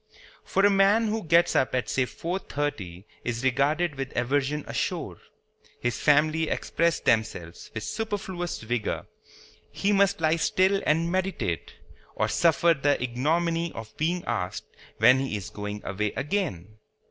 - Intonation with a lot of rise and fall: Yes, wide, 6.5 semitones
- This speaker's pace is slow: No, average, 145 wpm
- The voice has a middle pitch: Yes, medium, 150 Hz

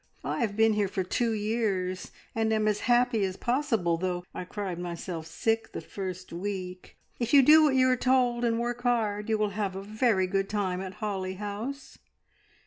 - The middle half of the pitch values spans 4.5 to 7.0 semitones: No, average, 4.1 semitones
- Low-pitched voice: No, high, 210 Hz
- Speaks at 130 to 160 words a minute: No, average, 195 wpm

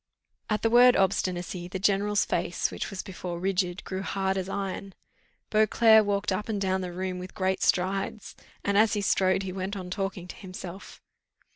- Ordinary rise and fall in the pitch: No, narrow, 1.5 semitones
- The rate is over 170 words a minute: Yes, average, 180 wpm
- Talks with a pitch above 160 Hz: Yes, high, 190 Hz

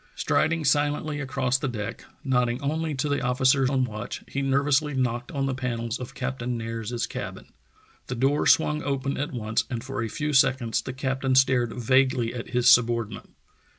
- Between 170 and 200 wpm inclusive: Yes, average, 175 wpm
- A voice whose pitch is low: Yes, low, 130 Hz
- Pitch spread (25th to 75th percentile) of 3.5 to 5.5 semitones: No, narrow, 2.4 semitones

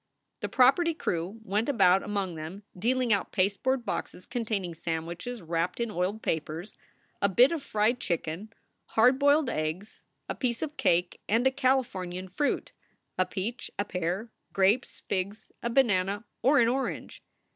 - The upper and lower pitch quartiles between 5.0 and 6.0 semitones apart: Yes, average, 5.3 semitones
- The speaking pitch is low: No, high, 205 Hz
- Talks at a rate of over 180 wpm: No, average, 150 wpm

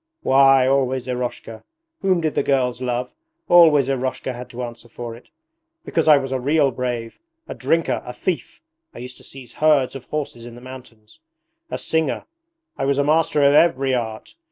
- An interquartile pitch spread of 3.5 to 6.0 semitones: No, average, 2.7 semitones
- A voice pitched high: No, low, 130 Hz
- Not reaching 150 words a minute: No, average, 180 wpm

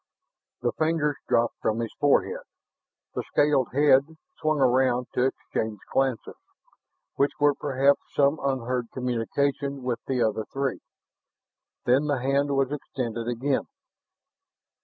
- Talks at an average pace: No, slow, 120 wpm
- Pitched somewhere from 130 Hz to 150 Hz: Yes, low, 135 Hz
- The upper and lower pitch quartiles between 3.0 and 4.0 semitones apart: No, narrow, 2.6 semitones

